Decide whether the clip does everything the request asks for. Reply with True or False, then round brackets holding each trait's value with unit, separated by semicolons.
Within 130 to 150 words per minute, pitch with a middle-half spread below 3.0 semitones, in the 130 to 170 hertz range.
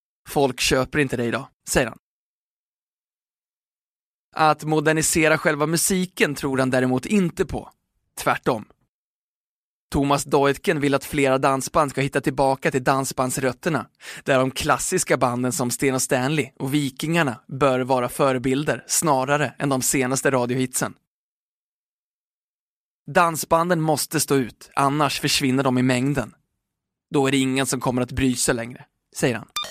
True (135 wpm; 2.5 semitones; 140 Hz)